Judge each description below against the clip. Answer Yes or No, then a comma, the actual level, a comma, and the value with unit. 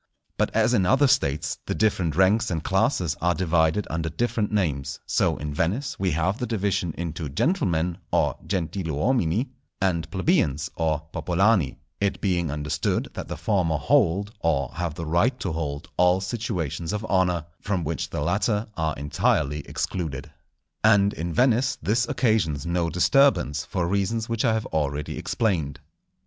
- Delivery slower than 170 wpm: Yes, average, 150 wpm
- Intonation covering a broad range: No, average, 4.8 semitones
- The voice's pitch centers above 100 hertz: No, very low, 90 Hz